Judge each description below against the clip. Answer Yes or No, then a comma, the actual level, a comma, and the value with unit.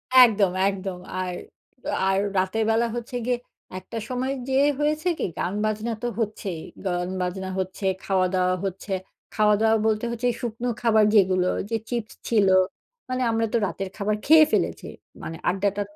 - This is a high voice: Yes, high, 210 Hz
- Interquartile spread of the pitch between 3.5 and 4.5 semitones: Yes, average, 3.8 semitones